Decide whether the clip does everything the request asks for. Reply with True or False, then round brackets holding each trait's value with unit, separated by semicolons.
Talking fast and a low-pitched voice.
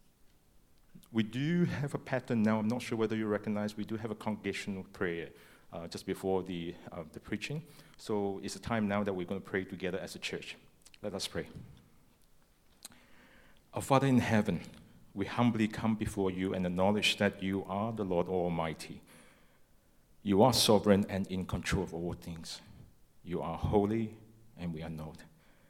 False (175 wpm; 100 Hz)